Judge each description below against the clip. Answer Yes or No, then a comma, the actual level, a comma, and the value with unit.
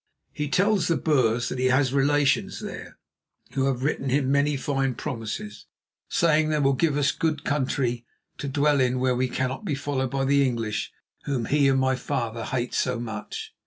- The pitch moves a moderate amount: No, narrow, 2.3 semitones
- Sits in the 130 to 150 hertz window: Yes, low, 135 Hz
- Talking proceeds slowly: No, average, 185 wpm